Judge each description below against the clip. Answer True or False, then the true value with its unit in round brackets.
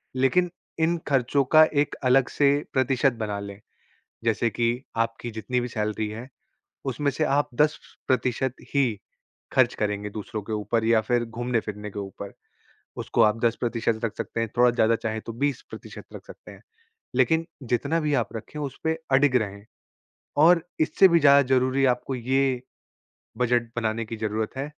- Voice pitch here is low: True (120 Hz)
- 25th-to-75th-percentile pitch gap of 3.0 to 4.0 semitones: True (3.7 semitones)